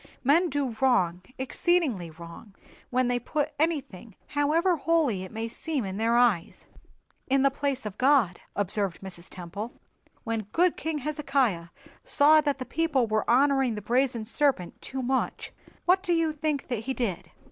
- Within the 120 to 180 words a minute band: Yes, average, 160 wpm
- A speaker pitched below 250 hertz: No, very high, 255 Hz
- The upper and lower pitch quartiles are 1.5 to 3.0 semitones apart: No, wide, 5.5 semitones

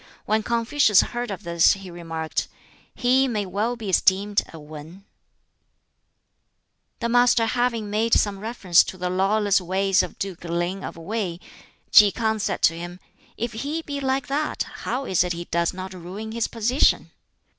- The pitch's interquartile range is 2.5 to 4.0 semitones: No, average, 4.6 semitones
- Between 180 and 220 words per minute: No, average, 165 wpm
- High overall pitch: Yes, high, 205 Hz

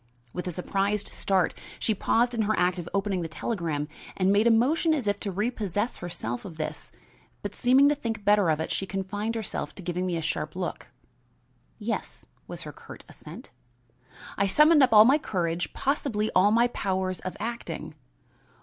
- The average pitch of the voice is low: No, high, 200 Hz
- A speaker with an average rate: Yes, average, 185 wpm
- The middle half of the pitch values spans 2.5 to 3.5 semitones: No, average, 4.1 semitones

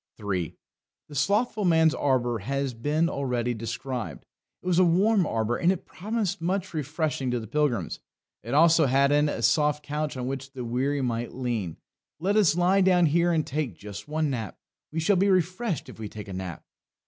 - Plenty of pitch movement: Yes, wide, 6.0 semitones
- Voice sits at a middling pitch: Yes, medium, 145 Hz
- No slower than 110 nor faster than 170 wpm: No, average, 195 wpm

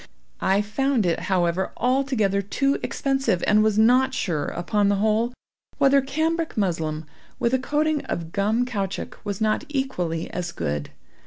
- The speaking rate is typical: Yes, average, 150 wpm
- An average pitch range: No, wide, 6.1 semitones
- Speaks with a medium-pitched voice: No, high, 215 Hz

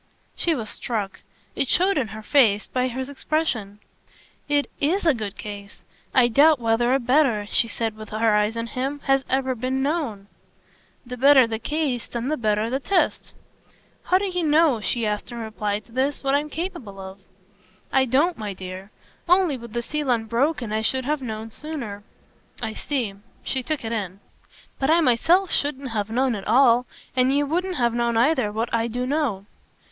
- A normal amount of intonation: Yes, average, 4.7 semitones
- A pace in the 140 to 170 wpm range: No, average, 185 wpm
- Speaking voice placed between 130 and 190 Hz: No, high, 245 Hz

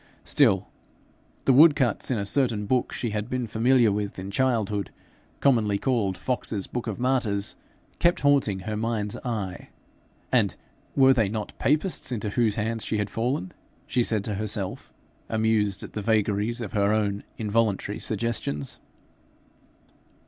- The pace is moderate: Yes, average, 150 wpm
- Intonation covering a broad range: No, average, 3.2 semitones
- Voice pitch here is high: No, low, 110 Hz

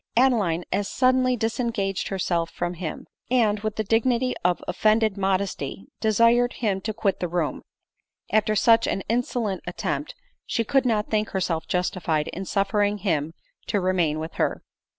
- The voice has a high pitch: Yes, high, 205 Hz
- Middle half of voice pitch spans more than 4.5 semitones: No, average, 4.0 semitones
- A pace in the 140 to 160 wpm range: Yes, average, 155 wpm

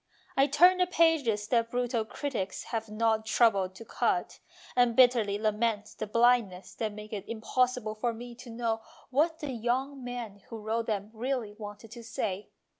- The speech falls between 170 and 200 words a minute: Yes, average, 175 wpm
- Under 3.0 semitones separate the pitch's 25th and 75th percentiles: Yes, narrow, 2.6 semitones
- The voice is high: Yes, high, 230 Hz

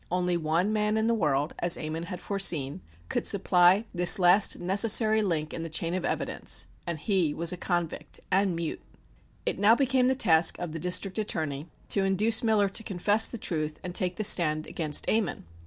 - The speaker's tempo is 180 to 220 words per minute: Yes, average, 190 wpm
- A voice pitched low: No, medium, 180 Hz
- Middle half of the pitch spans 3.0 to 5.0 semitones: Yes, average, 3.9 semitones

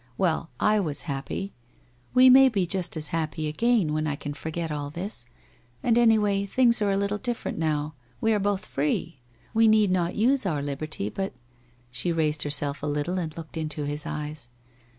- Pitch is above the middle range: No, medium, 165 Hz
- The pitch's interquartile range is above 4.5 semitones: Yes, wide, 5.5 semitones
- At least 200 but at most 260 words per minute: No, average, 190 wpm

